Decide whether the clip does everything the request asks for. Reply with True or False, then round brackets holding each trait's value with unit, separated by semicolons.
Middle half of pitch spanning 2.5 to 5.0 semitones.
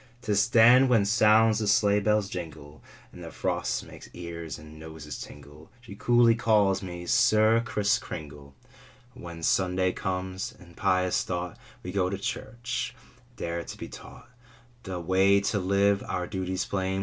True (3.5 semitones)